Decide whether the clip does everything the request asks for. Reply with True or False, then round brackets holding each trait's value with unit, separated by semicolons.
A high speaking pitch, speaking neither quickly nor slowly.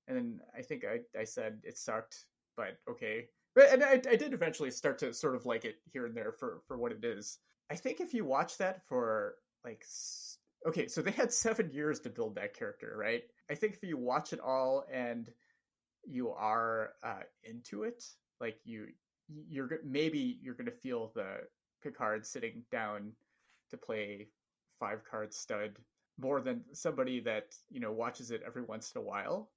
True (215 Hz; 185 wpm)